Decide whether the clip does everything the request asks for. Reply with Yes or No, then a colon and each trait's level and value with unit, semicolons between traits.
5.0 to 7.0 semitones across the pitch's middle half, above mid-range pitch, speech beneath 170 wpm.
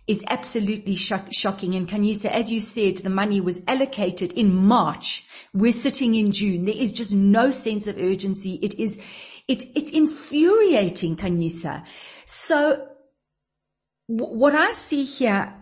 Yes: wide, 5.4 semitones; high, 215 Hz; average, 150 wpm